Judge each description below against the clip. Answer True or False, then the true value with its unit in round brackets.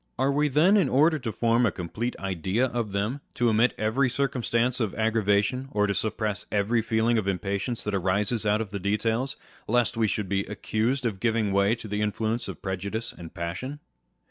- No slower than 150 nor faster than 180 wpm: False (195 wpm)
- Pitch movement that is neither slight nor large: True (3.3 semitones)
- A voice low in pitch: True (110 Hz)